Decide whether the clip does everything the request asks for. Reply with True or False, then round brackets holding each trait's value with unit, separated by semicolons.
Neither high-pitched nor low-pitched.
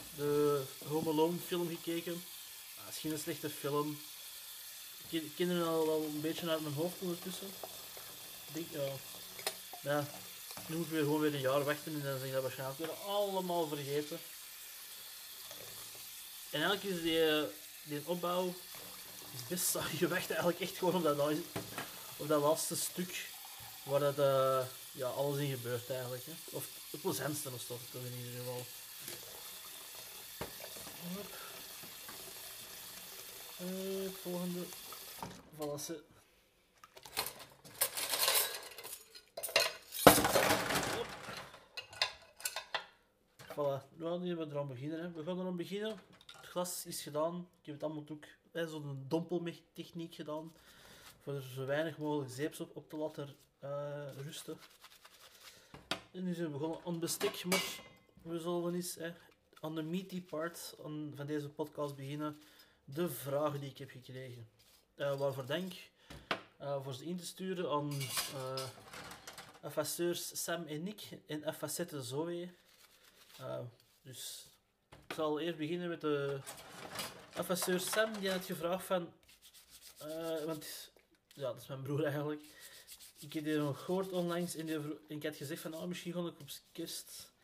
True (155 Hz)